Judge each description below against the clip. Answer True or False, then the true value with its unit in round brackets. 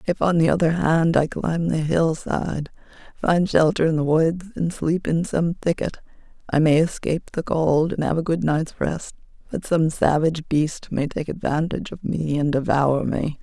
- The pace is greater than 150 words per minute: True (190 wpm)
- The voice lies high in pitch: False (160 Hz)